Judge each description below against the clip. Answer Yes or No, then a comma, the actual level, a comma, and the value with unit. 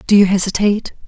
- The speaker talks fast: No, average, 170 wpm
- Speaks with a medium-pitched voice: No, high, 200 Hz